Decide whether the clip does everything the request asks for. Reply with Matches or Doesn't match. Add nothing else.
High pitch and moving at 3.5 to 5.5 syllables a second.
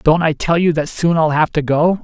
Doesn't match